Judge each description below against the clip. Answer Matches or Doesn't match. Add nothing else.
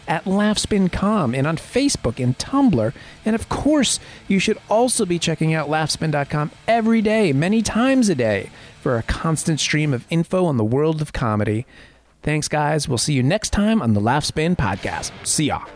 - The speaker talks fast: Doesn't match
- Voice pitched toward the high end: Doesn't match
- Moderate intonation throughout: Doesn't match